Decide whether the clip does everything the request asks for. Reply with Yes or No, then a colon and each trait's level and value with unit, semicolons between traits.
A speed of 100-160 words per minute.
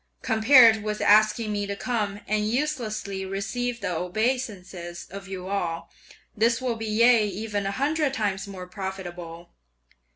Yes: average, 140 wpm